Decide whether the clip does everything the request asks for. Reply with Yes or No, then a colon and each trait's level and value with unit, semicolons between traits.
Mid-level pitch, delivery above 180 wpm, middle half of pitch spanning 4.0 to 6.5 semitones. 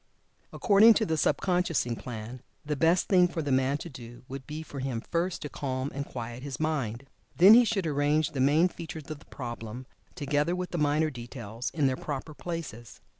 Yes: medium, 145 Hz; average, 200 wpm; average, 4.4 semitones